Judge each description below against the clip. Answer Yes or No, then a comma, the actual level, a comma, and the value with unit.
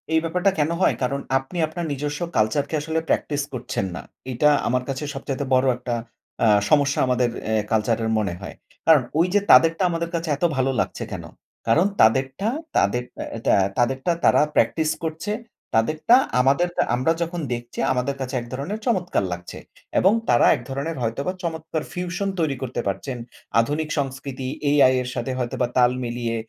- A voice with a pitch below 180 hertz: Yes, low, 135 Hz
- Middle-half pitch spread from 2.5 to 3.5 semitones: No, average, 4.7 semitones